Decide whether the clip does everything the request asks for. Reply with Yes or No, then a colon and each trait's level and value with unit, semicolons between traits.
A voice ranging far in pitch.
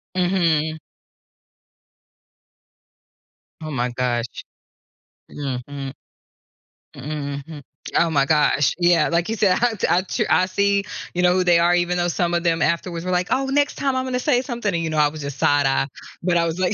No: average, 3.9 semitones